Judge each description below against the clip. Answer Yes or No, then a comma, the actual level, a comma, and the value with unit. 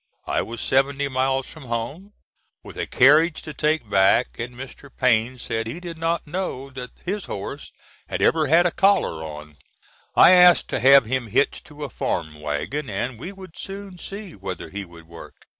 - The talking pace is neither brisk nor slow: Yes, average, 185 wpm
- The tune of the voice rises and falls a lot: Yes, wide, 6.8 semitones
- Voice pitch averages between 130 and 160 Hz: Yes, low, 135 Hz